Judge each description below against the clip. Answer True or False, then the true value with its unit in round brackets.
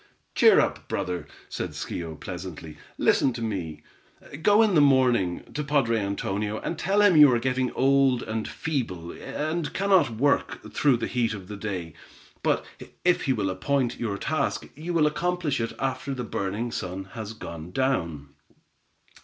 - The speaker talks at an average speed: True (160 wpm)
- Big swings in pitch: True (6.6 semitones)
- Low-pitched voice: True (125 Hz)